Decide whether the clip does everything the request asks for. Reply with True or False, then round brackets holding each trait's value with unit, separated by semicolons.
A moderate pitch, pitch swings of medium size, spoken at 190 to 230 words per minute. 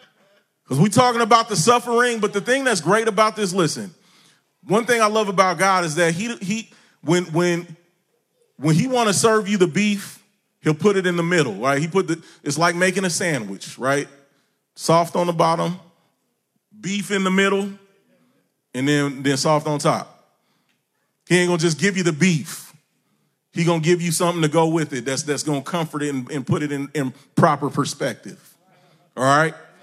True (175 Hz; 4.3 semitones; 200 wpm)